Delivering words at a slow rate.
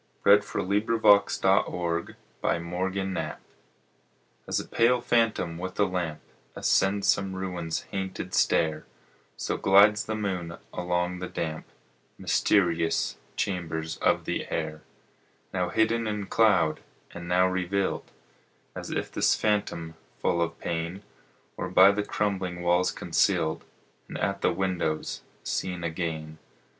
Yes: slow, 120 wpm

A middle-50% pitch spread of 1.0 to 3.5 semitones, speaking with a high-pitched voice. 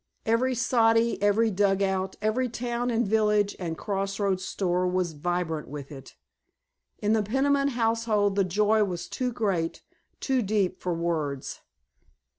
No: average, 3.9 semitones; high, 205 Hz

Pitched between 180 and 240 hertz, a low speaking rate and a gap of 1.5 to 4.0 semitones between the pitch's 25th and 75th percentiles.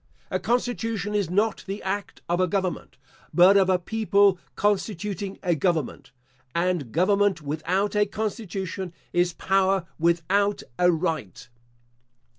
Yes: high, 190 Hz; slow, 125 wpm; average, 2.8 semitones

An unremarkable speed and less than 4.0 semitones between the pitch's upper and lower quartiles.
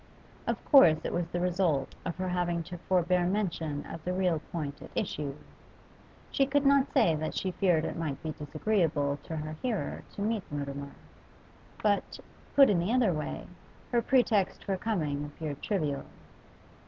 No: average, 165 wpm; average, 4.7 semitones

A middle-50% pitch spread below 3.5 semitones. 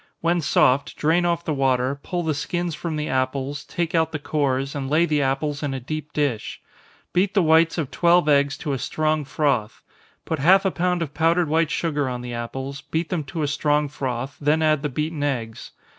Yes: average, 3.1 semitones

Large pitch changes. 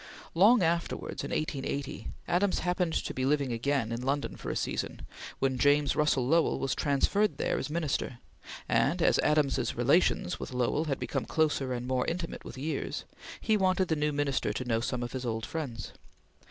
No: average, 4.1 semitones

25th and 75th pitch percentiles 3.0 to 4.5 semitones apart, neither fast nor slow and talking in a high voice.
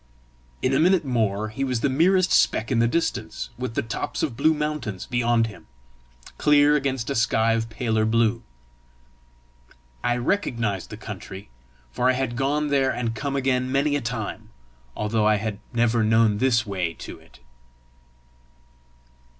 No: average, 3.7 semitones; average, 160 wpm; low, 120 Hz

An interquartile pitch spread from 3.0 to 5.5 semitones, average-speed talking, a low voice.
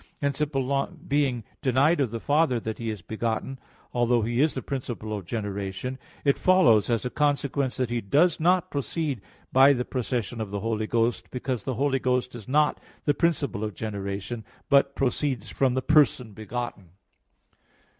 Yes: average, 4.1 semitones; average, 170 wpm; low, 125 Hz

